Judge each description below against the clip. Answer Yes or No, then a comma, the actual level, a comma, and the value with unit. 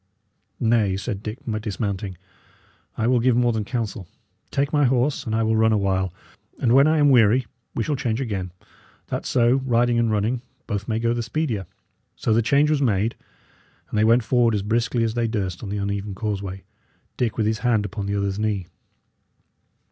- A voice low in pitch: Yes, low, 110 Hz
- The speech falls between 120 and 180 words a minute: No, average, 190 wpm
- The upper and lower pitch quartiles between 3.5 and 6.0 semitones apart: No, average, 3.0 semitones